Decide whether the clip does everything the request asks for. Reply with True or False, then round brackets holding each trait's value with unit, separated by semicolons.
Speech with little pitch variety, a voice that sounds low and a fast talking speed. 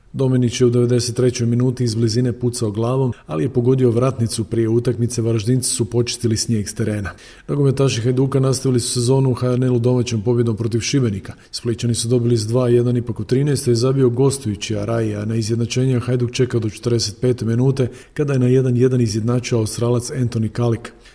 True (1.7 semitones; 120 Hz; 175 wpm)